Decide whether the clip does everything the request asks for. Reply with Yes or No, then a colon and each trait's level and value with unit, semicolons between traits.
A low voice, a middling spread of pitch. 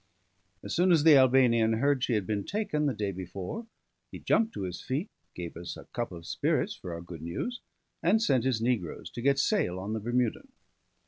No: low, 120 Hz; wide, 7.2 semitones